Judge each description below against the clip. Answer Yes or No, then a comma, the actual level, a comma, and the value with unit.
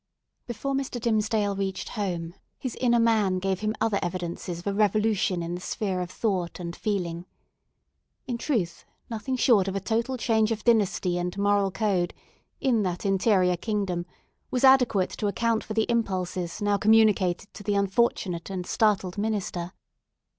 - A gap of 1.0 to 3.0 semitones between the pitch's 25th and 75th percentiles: No, average, 3.5 semitones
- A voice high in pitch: Yes, high, 200 Hz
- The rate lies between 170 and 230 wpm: No, average, 160 wpm